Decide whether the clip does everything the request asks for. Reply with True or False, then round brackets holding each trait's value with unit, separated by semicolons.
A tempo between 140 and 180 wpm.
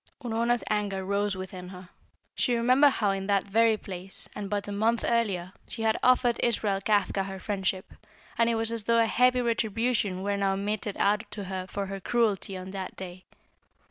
False (190 wpm)